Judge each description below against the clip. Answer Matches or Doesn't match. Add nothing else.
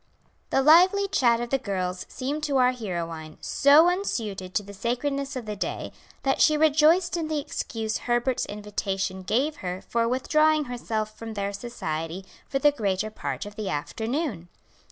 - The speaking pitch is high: Matches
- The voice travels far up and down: Matches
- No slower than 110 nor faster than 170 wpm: Matches